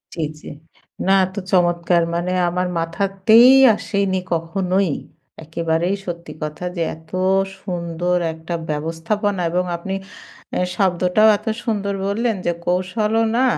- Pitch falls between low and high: Yes, medium, 180 Hz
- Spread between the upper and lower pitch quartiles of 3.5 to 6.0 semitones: No, average, 2.9 semitones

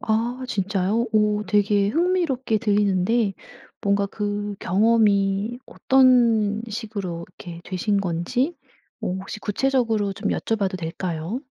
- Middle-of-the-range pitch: No, high, 210 Hz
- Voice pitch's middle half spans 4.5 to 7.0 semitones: No, average, 2.9 semitones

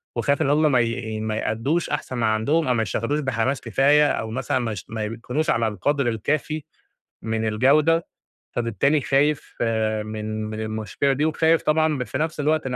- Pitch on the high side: No, low, 125 Hz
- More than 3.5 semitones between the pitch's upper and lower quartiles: Yes, average, 5.2 semitones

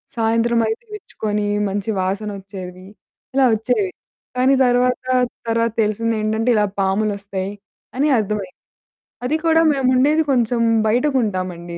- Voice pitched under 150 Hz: No, high, 220 Hz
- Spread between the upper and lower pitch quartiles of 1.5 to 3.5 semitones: No, average, 4.0 semitones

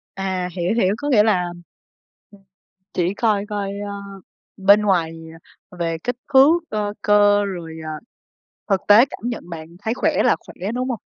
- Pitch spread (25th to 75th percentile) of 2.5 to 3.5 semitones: Yes, average, 3.2 semitones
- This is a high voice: Yes, high, 205 Hz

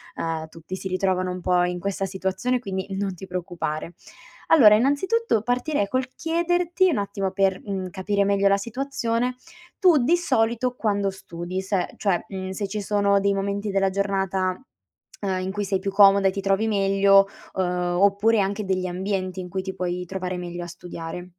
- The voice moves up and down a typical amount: No, narrow, 2.2 semitones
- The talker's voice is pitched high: Yes, high, 195 Hz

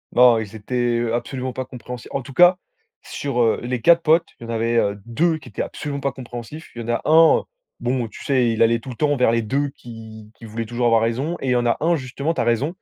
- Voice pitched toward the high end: No, low, 125 Hz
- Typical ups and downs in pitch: Yes, average, 3.5 semitones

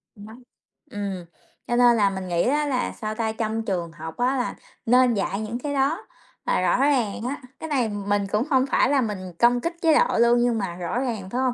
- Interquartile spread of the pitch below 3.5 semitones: No, average, 4.1 semitones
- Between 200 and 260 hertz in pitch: Yes, high, 235 Hz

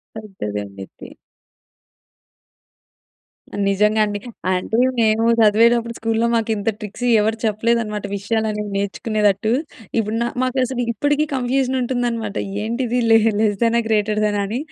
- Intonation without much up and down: Yes, narrow, 2.0 semitones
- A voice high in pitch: Yes, high, 220 Hz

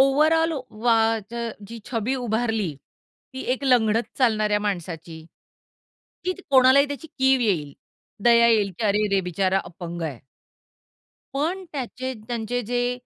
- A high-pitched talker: Yes, high, 230 Hz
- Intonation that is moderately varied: Yes, average, 4.3 semitones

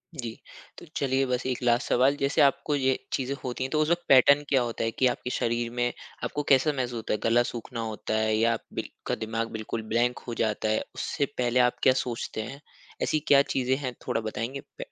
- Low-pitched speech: Yes, low, 125 Hz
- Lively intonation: No, average, 2.7 semitones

